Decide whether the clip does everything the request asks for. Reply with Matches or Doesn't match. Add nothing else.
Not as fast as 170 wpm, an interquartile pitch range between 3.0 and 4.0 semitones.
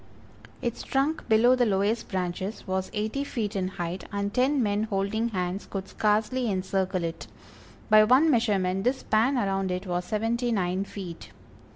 Matches